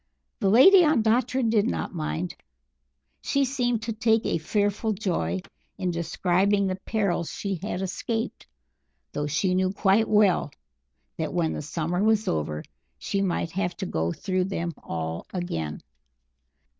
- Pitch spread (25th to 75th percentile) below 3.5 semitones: No, average, 4.6 semitones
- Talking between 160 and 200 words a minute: No, average, 145 wpm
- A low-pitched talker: No, high, 190 Hz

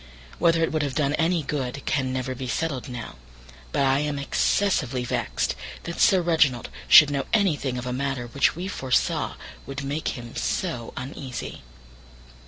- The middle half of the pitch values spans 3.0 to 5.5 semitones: Yes, average, 3.7 semitones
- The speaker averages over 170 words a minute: No, average, 165 wpm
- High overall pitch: No, medium, 140 Hz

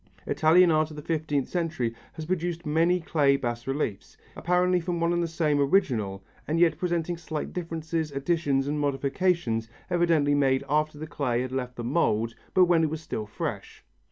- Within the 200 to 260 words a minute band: No, average, 180 wpm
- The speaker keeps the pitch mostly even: No, average, 3.7 semitones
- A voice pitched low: No, medium, 155 Hz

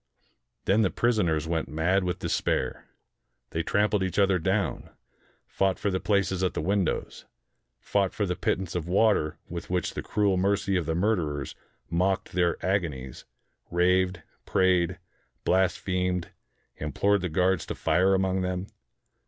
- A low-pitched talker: Yes, very low, 90 Hz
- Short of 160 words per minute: Yes, average, 145 wpm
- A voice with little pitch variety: Yes, narrow, 2.2 semitones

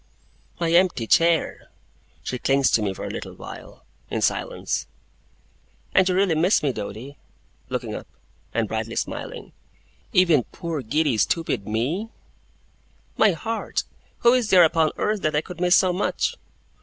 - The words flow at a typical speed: Yes, average, 150 wpm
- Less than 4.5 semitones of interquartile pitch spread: No, wide, 5.4 semitones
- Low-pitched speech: No, medium, 165 Hz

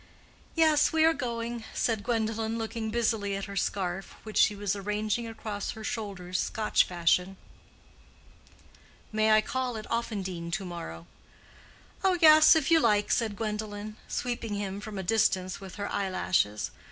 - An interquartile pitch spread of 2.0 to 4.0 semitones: Yes, average, 2.8 semitones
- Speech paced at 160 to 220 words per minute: No, average, 150 wpm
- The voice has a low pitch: No, high, 215 Hz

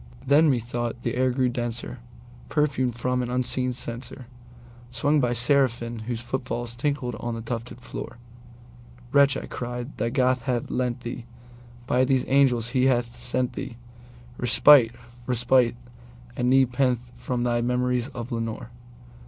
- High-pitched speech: No, low, 120 Hz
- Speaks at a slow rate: Yes, slow, 130 wpm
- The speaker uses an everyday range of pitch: No, narrow, 1.1 semitones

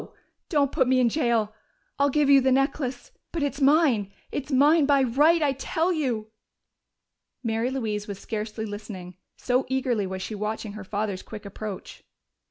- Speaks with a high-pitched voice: Yes, high, 245 Hz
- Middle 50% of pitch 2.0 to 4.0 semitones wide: No, average, 4.8 semitones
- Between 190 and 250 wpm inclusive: No, average, 165 wpm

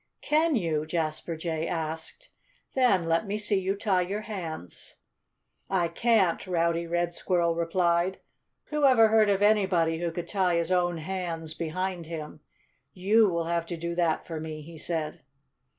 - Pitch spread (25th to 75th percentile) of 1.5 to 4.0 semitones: Yes, average, 2.8 semitones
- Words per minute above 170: No, average, 160 wpm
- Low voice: No, medium, 175 Hz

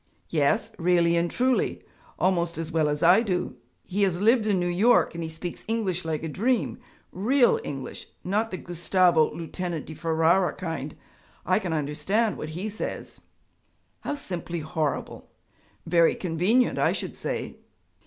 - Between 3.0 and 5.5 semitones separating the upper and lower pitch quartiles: Yes, average, 3.8 semitones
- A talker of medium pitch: Yes, medium, 175 Hz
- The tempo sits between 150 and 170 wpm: Yes, average, 155 wpm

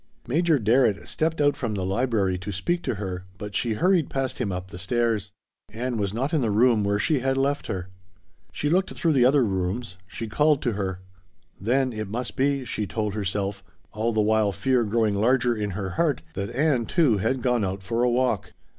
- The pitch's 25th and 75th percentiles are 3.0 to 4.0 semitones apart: No, average, 4.7 semitones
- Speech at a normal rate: No, fast, 210 wpm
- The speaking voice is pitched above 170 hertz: No, low, 115 Hz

